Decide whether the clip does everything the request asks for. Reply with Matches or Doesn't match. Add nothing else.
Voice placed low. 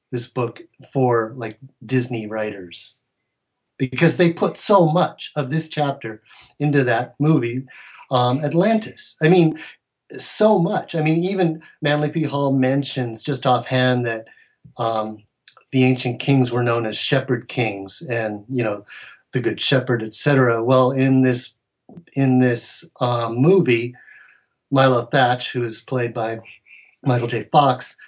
Matches